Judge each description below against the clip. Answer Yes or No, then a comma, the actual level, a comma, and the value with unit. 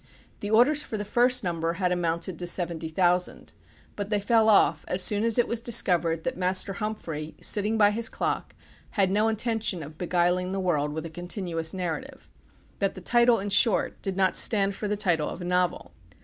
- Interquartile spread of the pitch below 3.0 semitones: No, average, 3.8 semitones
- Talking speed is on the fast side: No, average, 195 wpm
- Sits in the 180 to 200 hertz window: Yes, high, 190 Hz